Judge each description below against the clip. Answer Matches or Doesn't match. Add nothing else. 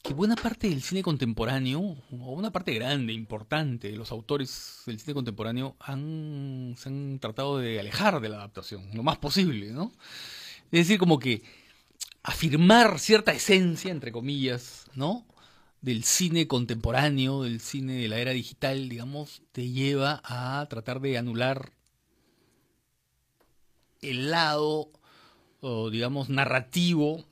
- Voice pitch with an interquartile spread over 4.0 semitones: Matches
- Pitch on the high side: Doesn't match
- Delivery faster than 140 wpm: Doesn't match